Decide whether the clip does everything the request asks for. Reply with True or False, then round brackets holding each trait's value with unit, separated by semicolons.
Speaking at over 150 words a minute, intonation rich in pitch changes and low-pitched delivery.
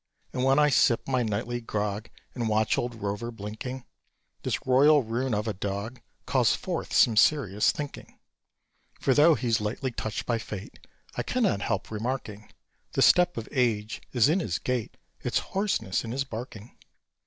False (165 wpm; 3.7 semitones; 115 Hz)